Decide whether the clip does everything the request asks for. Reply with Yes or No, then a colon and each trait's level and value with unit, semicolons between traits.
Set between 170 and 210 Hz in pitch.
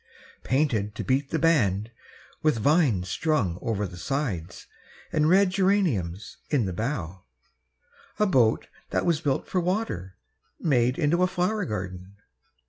No: low, 130 Hz